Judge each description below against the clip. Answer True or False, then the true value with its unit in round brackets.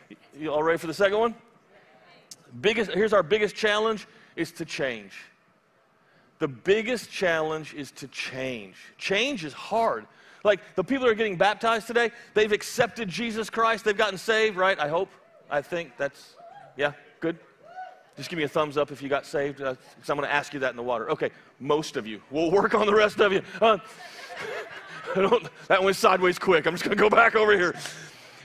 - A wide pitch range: True (7.0 semitones)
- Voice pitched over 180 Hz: True (190 Hz)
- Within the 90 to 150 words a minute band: False (195 wpm)